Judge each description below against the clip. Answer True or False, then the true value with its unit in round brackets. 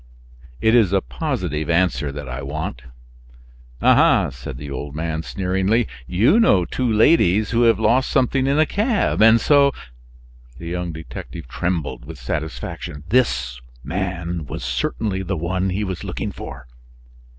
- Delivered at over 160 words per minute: False (150 wpm)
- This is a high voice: False (90 Hz)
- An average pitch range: False (7.4 semitones)